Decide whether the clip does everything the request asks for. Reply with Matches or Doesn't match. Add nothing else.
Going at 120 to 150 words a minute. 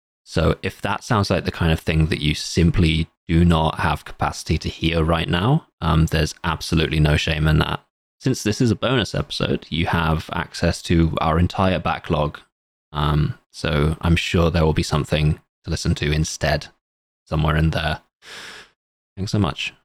Doesn't match